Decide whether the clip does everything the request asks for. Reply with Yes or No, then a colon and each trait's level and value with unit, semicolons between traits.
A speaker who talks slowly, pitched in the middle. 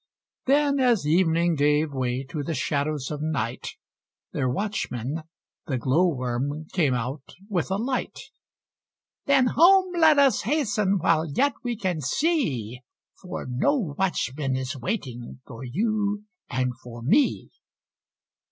Yes: slow, 125 wpm; medium, 160 Hz